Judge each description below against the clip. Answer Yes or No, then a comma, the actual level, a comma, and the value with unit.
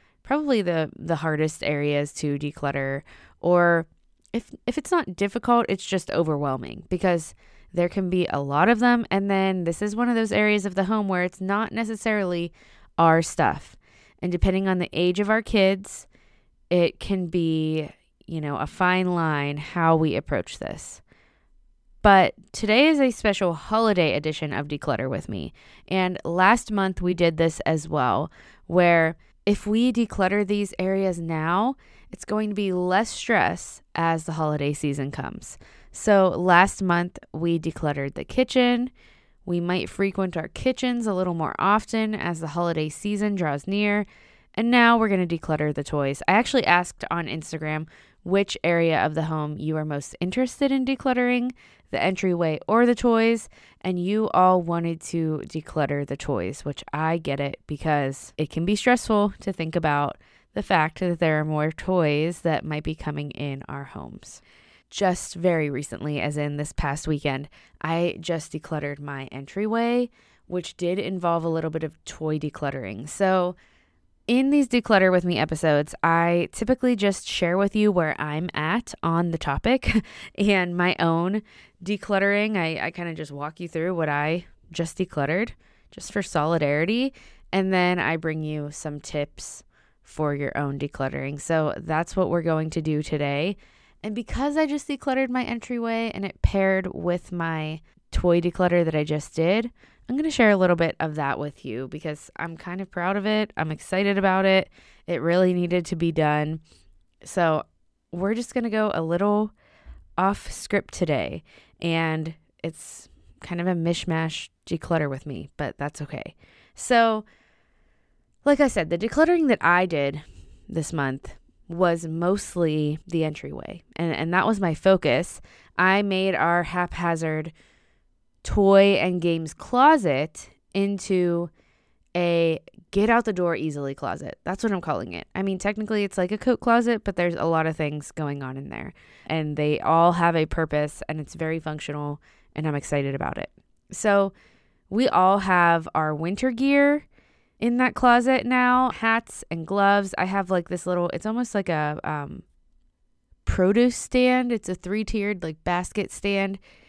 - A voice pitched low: No, medium, 175 Hz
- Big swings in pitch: No, average, 4.7 semitones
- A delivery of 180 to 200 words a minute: No, average, 170 wpm